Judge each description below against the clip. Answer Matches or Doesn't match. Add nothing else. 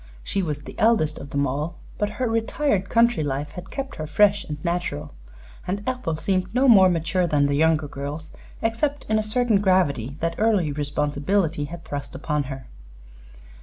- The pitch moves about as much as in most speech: Doesn't match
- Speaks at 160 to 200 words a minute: Matches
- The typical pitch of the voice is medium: Matches